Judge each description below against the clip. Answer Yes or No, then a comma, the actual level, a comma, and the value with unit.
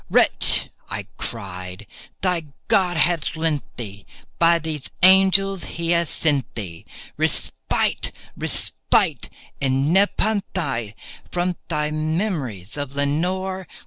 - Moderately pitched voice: Yes, medium, 160 Hz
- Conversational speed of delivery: No, slow, 95 wpm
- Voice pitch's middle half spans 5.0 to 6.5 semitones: Yes, wide, 5.6 semitones